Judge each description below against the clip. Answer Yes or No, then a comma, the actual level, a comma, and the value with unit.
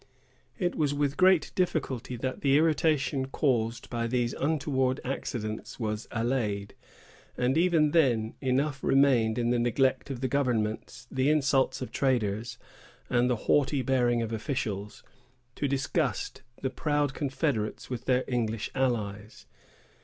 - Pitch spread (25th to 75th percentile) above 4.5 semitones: No, average, 3.3 semitones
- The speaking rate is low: Yes, slow, 130 wpm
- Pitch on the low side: Yes, low, 130 Hz